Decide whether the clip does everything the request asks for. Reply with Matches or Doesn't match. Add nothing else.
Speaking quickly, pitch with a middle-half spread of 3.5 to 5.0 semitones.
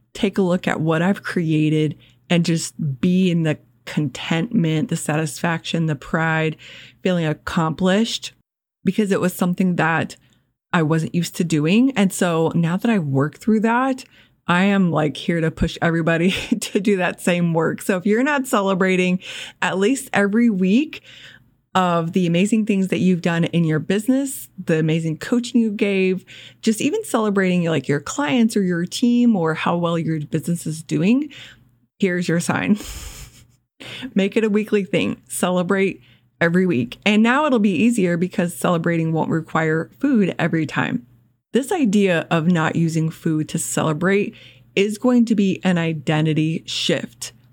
Doesn't match